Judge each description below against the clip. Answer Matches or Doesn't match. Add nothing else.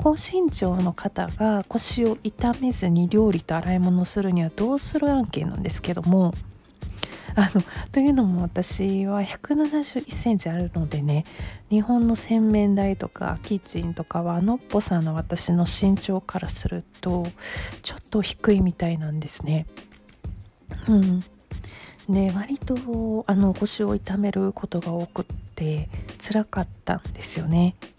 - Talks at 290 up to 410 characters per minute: Doesn't match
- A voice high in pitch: Matches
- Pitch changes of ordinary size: Matches